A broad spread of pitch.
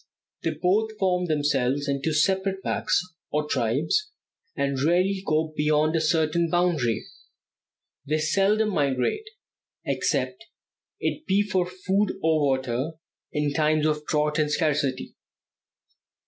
No: average, 4.0 semitones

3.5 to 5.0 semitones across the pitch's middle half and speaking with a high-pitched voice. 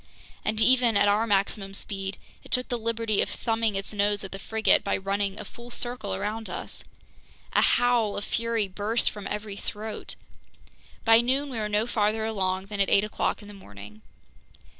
No: narrow, 2.4 semitones; high, 210 Hz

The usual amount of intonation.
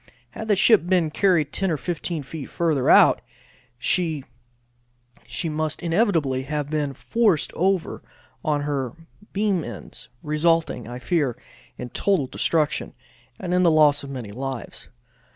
Yes: average, 4.1 semitones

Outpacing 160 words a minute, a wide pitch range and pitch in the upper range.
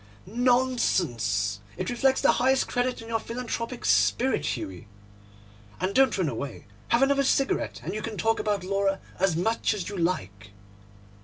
No: average, 155 wpm; wide, 6.3 semitones; high, 210 Hz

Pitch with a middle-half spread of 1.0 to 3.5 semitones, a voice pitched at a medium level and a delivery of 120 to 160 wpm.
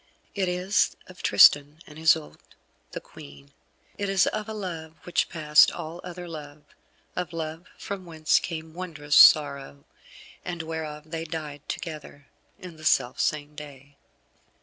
Yes: average, 3.0 semitones; medium, 160 Hz; average, 145 wpm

